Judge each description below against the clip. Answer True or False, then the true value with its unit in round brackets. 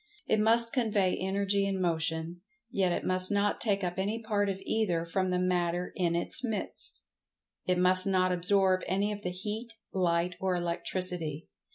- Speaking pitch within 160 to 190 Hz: True (185 Hz)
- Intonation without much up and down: True (2.3 semitones)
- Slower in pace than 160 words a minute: False (170 wpm)